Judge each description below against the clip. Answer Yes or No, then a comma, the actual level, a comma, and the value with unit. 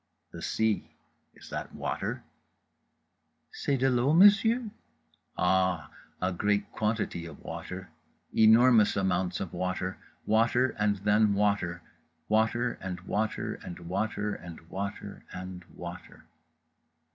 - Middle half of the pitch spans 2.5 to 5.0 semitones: Yes, average, 3.4 semitones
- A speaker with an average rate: No, slow, 110 wpm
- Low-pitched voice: Yes, low, 105 Hz